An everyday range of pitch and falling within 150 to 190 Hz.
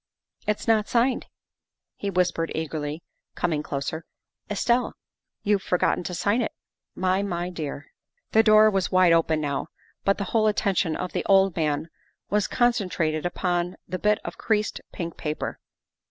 Yes: average, 4.3 semitones; medium, 185 Hz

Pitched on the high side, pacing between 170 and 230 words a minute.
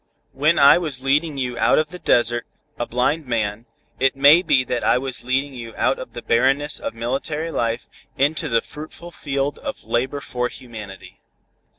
No: low, 135 Hz; average, 180 wpm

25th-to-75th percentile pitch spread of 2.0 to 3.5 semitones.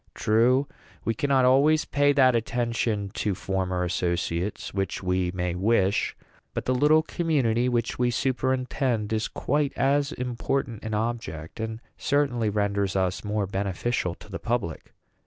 No: average, 4.8 semitones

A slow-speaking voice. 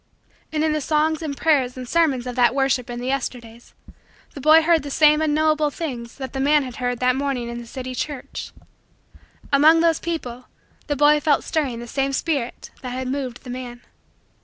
No: average, 195 wpm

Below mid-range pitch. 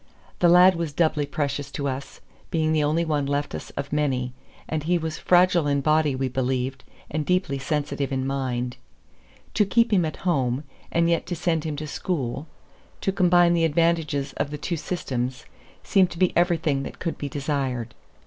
No: medium, 150 Hz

